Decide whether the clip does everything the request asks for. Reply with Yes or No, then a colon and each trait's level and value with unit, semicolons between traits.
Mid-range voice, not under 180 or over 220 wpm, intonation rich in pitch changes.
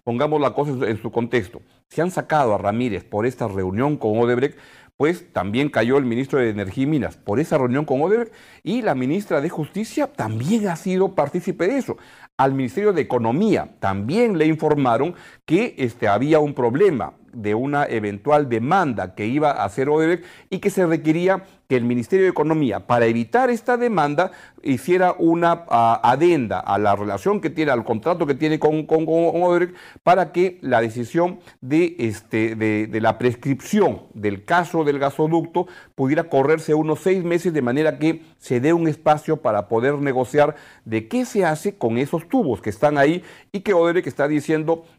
Yes: medium, 150 Hz; average, 185 wpm; wide, 6.1 semitones